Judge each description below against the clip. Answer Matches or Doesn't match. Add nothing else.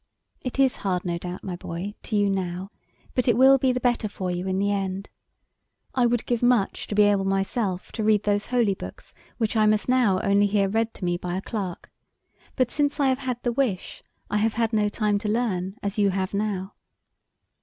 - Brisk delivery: Matches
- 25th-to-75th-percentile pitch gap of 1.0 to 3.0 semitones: Doesn't match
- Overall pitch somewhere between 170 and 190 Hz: Doesn't match